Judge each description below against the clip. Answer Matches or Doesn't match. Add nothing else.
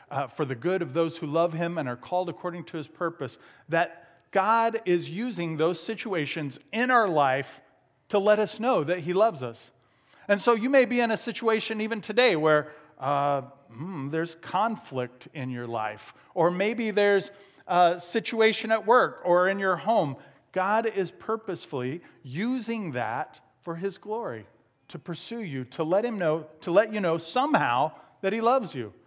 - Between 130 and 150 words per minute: Doesn't match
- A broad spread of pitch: Matches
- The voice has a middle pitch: Matches